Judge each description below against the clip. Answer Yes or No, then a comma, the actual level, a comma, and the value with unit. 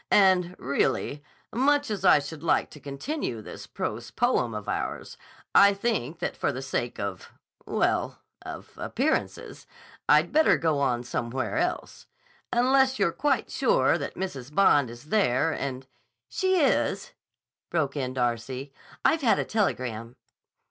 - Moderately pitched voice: Yes, medium, 150 Hz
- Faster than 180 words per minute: No, average, 140 wpm